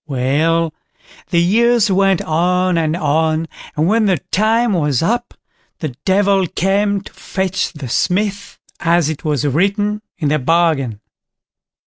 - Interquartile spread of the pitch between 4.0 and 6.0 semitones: Yes, average, 4.3 semitones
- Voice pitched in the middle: Yes, medium, 175 Hz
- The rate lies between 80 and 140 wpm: Yes, slow, 135 wpm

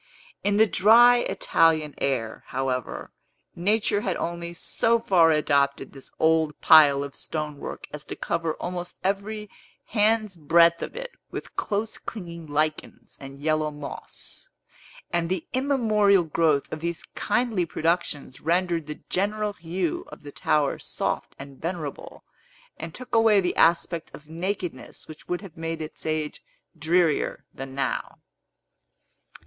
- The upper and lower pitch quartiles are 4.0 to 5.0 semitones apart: Yes, average, 4.7 semitones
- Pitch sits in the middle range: Yes, medium, 165 Hz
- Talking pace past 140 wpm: No, slow, 135 wpm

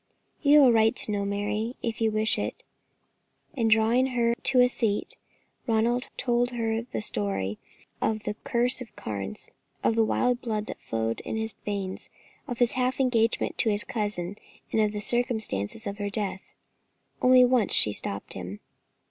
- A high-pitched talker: Yes, high, 220 Hz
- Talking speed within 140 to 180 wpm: Yes, average, 175 wpm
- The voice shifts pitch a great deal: No, average, 3.0 semitones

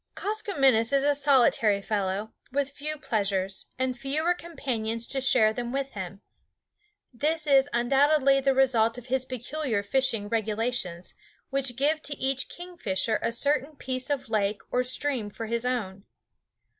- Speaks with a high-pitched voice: Yes, very high, 255 Hz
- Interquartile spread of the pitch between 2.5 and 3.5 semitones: No, average, 4.1 semitones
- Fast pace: No, average, 145 wpm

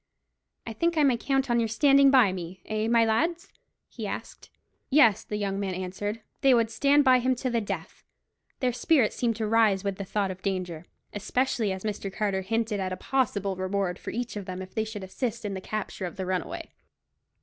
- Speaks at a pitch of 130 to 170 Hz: No, high, 215 Hz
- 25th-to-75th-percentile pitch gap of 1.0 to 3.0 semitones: No, average, 4.2 semitones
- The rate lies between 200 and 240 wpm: Yes, fast, 205 wpm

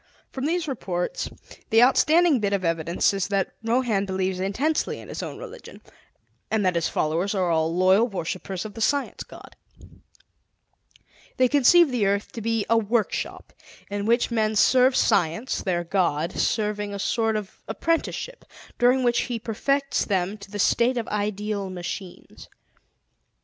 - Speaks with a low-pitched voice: No, high, 210 Hz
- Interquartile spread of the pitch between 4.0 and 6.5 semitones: Yes, average, 4.5 semitones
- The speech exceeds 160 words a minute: No, average, 155 wpm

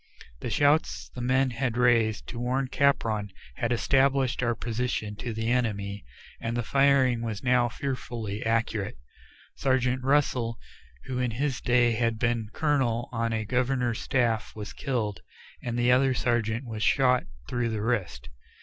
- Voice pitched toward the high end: No, low, 120 Hz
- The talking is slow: No, average, 155 wpm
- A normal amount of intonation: No, narrow, 2.3 semitones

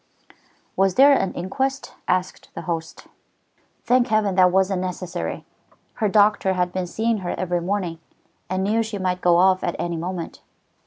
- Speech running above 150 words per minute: Yes, average, 160 wpm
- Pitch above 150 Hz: Yes, medium, 185 Hz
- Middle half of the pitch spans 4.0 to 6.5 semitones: No, average, 2.7 semitones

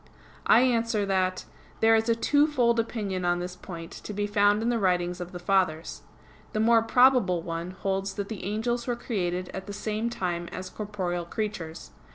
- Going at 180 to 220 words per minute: Yes, average, 185 wpm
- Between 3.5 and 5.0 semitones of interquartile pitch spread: Yes, average, 4.0 semitones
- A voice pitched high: Yes, high, 200 Hz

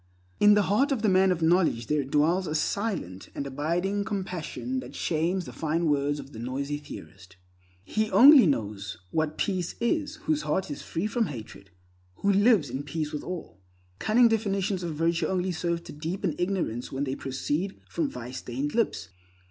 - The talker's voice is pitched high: No, medium, 170 Hz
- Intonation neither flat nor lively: No, wide, 5.9 semitones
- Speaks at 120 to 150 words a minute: No, average, 180 wpm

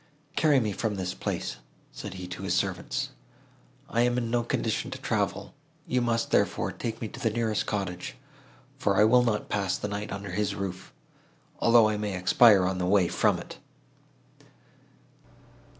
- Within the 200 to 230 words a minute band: No, average, 170 wpm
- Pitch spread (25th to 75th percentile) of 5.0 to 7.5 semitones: No, average, 3.2 semitones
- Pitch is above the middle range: No, low, 105 Hz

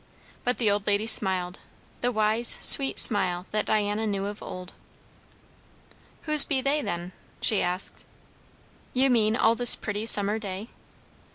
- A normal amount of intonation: Yes, average, 3.0 semitones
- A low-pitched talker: No, high, 210 Hz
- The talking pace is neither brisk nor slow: Yes, average, 145 wpm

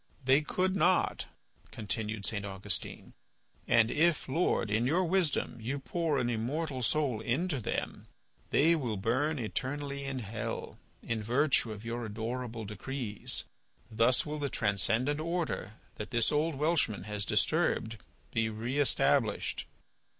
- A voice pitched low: Yes, low, 125 Hz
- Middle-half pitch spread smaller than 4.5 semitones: No, average, 5.2 semitones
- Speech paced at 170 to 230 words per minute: No, slow, 135 wpm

